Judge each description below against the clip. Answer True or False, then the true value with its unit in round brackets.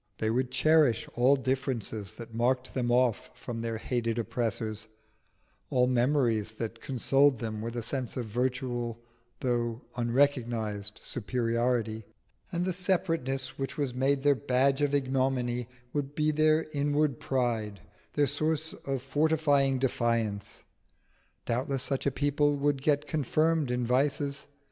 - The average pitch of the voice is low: True (130 Hz)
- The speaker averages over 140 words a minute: False (135 wpm)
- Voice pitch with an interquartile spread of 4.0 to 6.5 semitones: False (3.4 semitones)